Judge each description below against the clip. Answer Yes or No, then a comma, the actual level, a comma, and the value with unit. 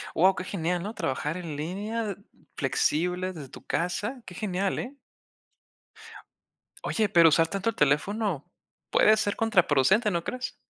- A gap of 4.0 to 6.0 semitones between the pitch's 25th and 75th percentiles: Yes, average, 4.5 semitones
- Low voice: No, medium, 185 Hz